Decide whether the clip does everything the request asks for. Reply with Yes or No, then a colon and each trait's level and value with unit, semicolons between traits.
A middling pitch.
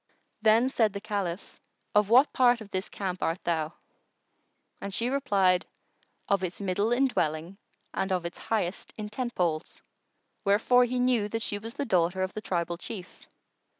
No: high, 200 Hz